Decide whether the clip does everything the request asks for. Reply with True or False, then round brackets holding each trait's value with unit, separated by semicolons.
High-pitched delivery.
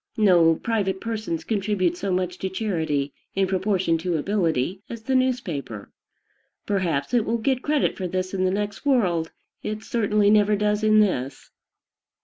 True (195 Hz)